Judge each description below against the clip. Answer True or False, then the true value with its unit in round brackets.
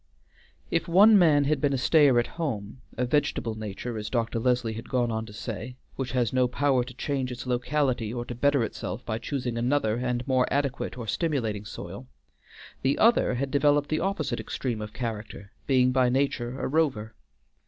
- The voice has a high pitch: False (125 Hz)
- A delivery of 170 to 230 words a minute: True (185 wpm)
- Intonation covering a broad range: False (3.6 semitones)